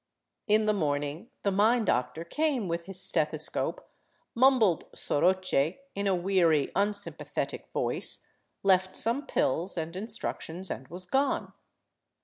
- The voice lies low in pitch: No, medium, 185 Hz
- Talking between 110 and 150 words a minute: Yes, slow, 135 wpm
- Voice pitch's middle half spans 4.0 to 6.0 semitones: Yes, average, 4.3 semitones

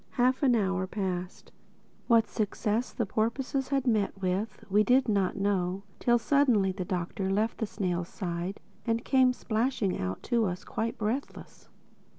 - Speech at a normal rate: Yes, average, 155 wpm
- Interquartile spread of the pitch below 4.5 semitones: Yes, average, 4.0 semitones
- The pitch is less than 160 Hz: No, high, 210 Hz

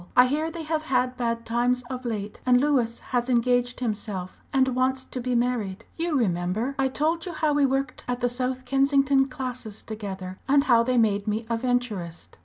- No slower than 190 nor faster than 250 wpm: Yes, average, 195 wpm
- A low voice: No, very high, 250 Hz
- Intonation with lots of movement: No, average, 2.8 semitones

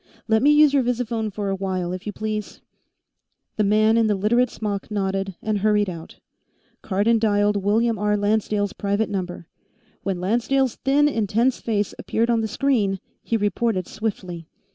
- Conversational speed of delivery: Yes, average, 165 wpm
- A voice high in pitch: Yes, high, 210 Hz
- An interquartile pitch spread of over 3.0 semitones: No, narrow, 2.4 semitones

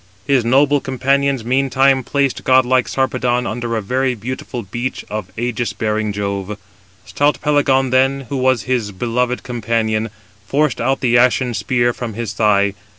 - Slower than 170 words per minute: Yes, average, 150 wpm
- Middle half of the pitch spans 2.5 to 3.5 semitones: Yes, average, 2.8 semitones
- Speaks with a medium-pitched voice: No, low, 125 Hz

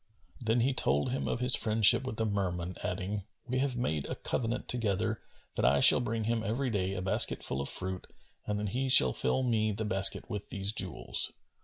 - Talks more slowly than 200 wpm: No, fast, 205 wpm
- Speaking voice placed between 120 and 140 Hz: No, low, 105 Hz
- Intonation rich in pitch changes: No, average, 4.2 semitones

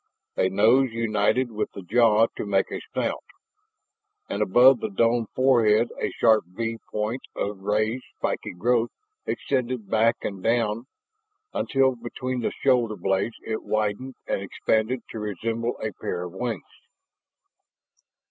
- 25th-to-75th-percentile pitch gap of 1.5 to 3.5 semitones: Yes, narrow, 2.6 semitones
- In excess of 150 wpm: No, average, 140 wpm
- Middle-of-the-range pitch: No, low, 115 Hz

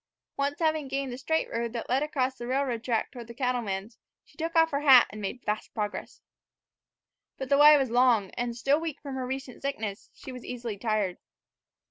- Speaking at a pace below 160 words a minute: No, average, 200 wpm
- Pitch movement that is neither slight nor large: Yes, average, 3.3 semitones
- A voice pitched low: No, very high, 255 Hz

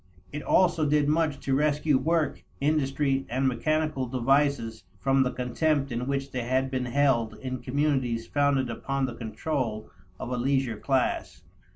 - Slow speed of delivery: No, average, 155 wpm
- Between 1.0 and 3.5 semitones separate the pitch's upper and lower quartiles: Yes, narrow, 2.6 semitones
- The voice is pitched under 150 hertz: Yes, low, 135 Hz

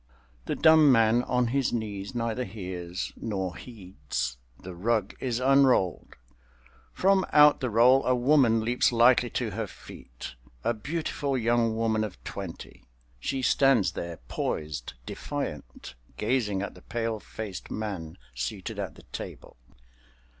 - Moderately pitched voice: No, low, 110 Hz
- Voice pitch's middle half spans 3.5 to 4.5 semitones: No, average, 5.1 semitones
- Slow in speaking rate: Yes, slow, 130 wpm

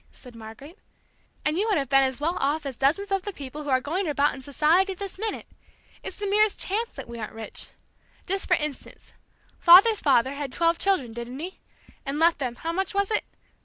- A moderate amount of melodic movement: No, wide, 6.1 semitones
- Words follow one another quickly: Yes, fast, 210 wpm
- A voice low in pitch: No, very high, 305 Hz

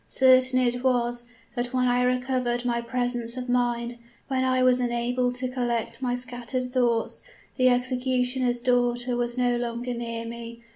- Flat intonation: Yes, narrow, 0.9 semitones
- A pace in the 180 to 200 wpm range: No, average, 155 wpm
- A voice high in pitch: Yes, high, 245 Hz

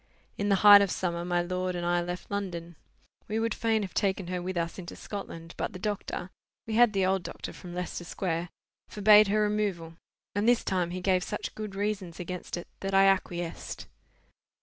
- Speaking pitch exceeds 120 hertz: Yes, medium, 185 Hz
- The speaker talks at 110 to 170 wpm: No, average, 195 wpm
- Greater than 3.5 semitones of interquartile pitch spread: No, average, 2.7 semitones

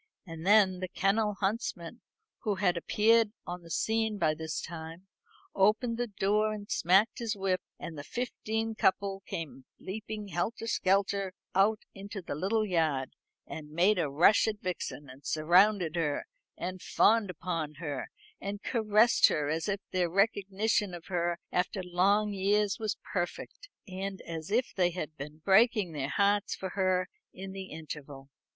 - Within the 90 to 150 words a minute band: No, average, 160 wpm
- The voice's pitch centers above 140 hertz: Yes, high, 190 Hz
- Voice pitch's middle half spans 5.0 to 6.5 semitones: No, average, 3.7 semitones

